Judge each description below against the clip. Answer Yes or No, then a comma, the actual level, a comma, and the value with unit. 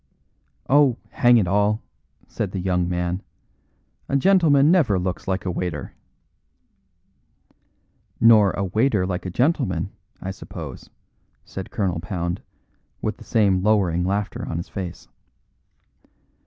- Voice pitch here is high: No, very low, 95 Hz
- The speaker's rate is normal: No, slow, 125 wpm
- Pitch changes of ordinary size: Yes, average, 4.2 semitones